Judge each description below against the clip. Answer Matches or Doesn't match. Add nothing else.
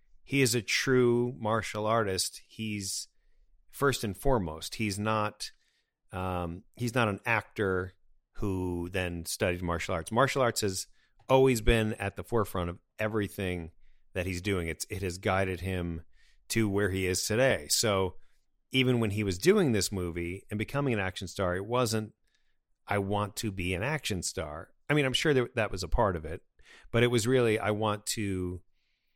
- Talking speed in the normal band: Matches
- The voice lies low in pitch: Matches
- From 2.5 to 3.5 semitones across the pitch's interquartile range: Doesn't match